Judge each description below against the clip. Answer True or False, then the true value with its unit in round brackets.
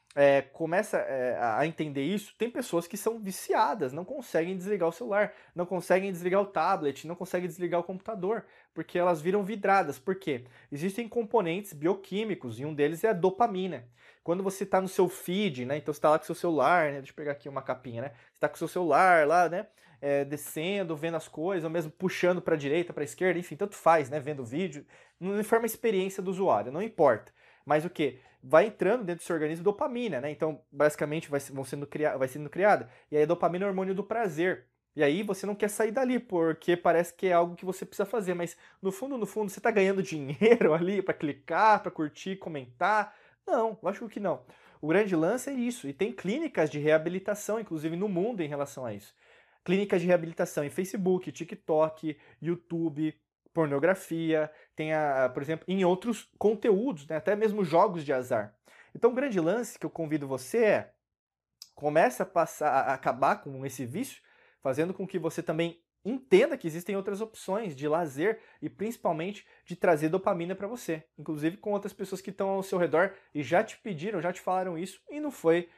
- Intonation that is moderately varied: True (4.3 semitones)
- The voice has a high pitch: False (175 Hz)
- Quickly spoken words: True (205 wpm)